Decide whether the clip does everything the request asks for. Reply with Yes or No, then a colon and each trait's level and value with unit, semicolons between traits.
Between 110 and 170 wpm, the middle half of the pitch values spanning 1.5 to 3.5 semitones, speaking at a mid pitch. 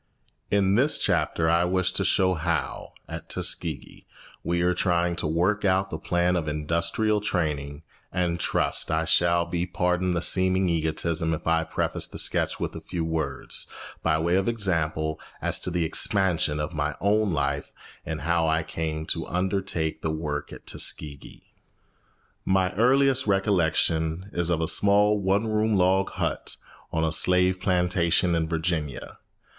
No: average, 160 wpm; average, 2.9 semitones; very low, 85 Hz